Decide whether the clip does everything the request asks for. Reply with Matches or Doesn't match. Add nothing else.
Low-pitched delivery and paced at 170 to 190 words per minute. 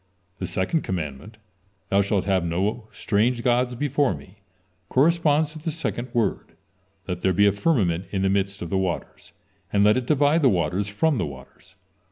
Matches